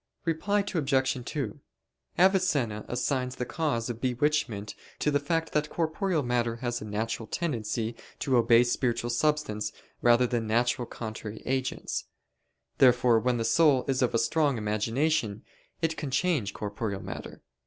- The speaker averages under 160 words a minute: Yes, average, 140 wpm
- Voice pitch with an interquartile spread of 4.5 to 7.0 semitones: Yes, average, 4.8 semitones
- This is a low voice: Yes, low, 125 Hz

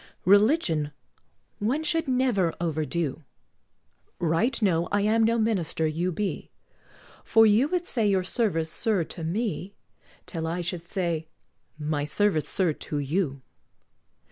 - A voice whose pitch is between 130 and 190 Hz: Yes, medium, 185 Hz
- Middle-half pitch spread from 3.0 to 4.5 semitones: No, wide, 5.4 semitones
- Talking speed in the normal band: No, slow, 130 wpm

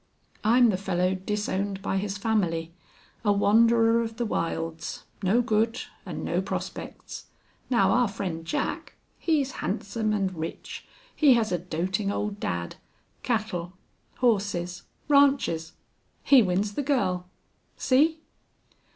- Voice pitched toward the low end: No, high, 205 Hz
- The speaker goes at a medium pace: No, slow, 125 wpm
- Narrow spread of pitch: No, average, 4.3 semitones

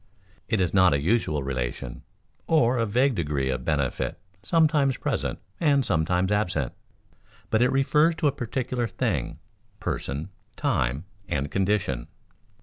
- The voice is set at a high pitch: No, low, 100 Hz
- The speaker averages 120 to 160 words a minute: Yes, slow, 135 wpm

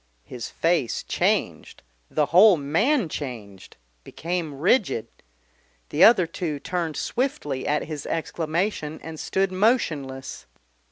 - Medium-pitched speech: Yes, medium, 160 Hz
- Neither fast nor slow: No, slow, 110 wpm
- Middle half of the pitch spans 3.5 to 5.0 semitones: Yes, average, 4.5 semitones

